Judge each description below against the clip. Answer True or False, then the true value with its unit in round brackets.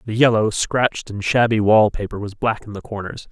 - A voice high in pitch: False (110 Hz)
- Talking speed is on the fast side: True (215 wpm)